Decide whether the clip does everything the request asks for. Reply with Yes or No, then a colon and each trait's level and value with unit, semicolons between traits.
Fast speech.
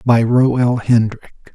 No: average, 155 wpm